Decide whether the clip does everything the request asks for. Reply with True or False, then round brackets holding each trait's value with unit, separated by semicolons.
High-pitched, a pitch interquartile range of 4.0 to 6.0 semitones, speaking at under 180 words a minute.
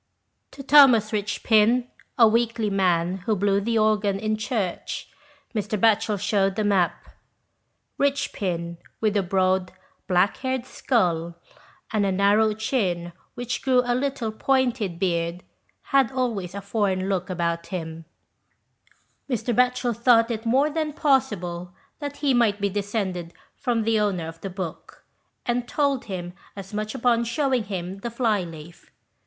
True (210 Hz; 4.5 semitones; 145 wpm)